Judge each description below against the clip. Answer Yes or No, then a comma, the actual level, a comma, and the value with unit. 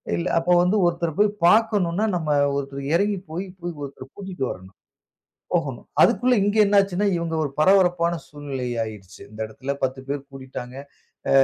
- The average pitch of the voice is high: No, medium, 170 Hz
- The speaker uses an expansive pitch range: Yes, wide, 6.3 semitones